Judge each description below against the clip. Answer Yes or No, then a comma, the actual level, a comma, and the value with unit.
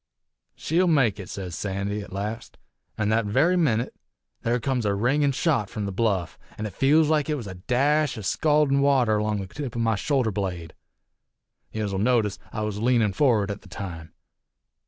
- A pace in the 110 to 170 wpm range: No, average, 185 wpm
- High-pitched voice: No, low, 110 Hz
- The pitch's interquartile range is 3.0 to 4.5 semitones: No, wide, 5.4 semitones